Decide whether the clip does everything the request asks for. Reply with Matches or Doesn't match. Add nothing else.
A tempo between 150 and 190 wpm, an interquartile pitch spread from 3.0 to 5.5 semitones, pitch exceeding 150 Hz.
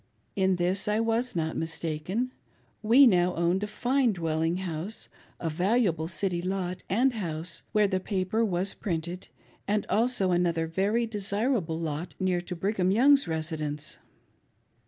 Doesn't match